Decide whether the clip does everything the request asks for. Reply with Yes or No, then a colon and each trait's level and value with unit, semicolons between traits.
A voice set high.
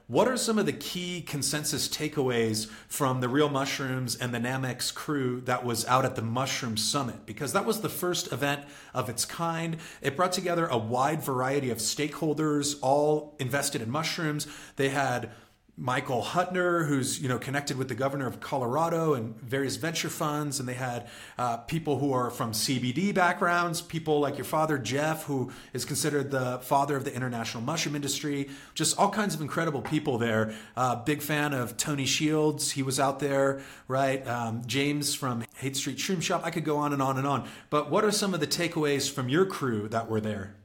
No: medium, 140 Hz